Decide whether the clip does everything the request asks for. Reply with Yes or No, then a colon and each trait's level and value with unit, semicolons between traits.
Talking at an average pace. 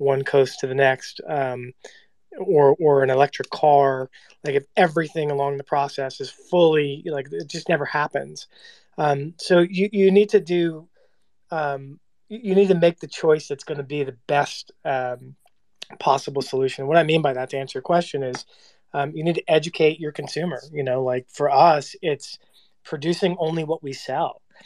Yes: average, 185 wpm